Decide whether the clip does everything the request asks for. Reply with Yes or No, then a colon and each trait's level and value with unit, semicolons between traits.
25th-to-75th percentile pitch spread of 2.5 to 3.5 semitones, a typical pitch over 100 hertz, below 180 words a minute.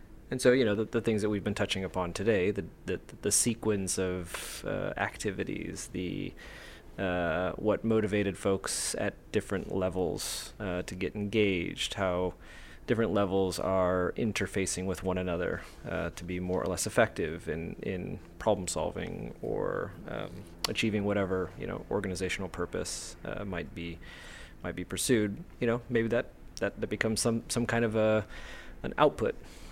No: average, 3.2 semitones; very low, 95 Hz; average, 160 wpm